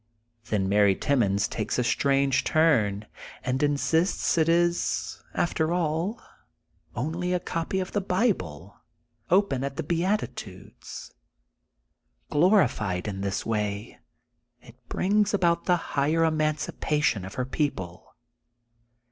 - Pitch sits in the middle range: Yes, medium, 145 Hz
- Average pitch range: No, wide, 8.3 semitones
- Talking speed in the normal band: No, slow, 115 wpm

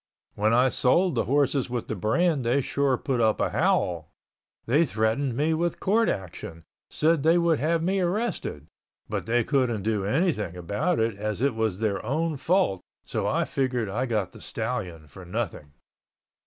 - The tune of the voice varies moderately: No, wide, 6.9 semitones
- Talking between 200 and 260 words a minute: No, average, 175 wpm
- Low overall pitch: Yes, low, 125 Hz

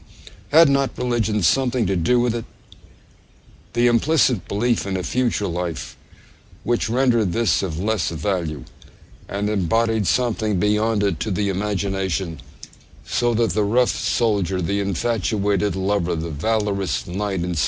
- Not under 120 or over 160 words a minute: Yes, average, 140 wpm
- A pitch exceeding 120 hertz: No, low, 105 Hz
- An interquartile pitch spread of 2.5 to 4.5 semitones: Yes, average, 3.8 semitones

